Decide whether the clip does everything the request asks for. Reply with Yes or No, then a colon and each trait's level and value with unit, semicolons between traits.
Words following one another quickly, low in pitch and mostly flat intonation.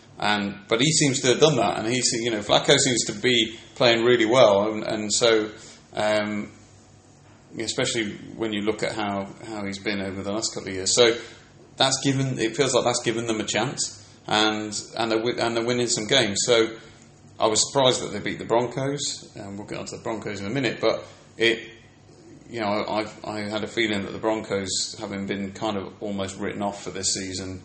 Yes: fast, 220 wpm; low, 110 Hz; narrow, 2.3 semitones